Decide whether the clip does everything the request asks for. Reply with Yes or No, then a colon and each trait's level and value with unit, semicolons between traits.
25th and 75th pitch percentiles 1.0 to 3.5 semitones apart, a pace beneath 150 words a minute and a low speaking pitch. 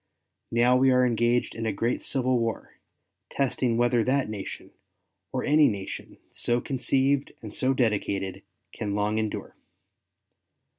Yes: average, 3.0 semitones; slow, 135 wpm; low, 120 Hz